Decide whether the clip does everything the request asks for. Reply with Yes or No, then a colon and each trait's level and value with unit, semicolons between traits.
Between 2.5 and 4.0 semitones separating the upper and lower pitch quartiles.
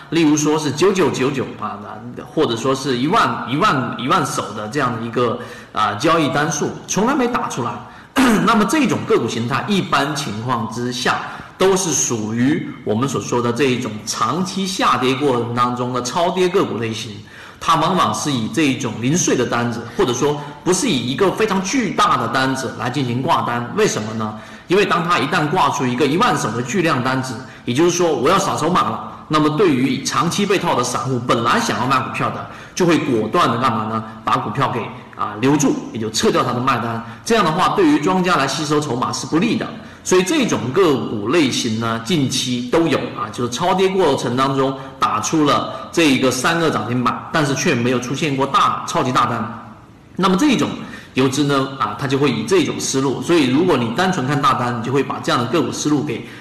No: average, 5.1 semitones